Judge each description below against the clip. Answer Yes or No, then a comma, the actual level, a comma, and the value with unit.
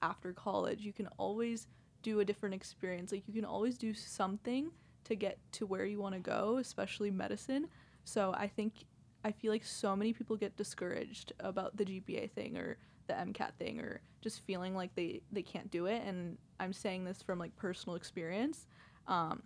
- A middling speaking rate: Yes, average, 190 wpm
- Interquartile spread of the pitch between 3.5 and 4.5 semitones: No, average, 2.7 semitones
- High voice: Yes, high, 205 Hz